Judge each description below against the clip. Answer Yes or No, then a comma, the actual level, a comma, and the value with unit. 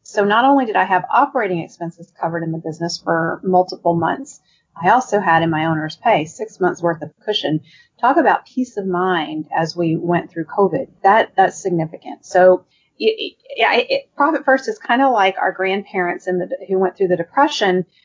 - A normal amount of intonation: Yes, average, 4.3 semitones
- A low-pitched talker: No, medium, 185 Hz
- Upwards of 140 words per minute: Yes, average, 200 wpm